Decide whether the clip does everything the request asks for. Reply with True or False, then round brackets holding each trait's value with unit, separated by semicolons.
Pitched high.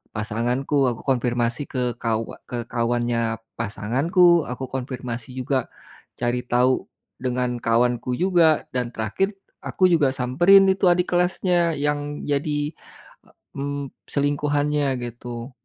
False (130 Hz)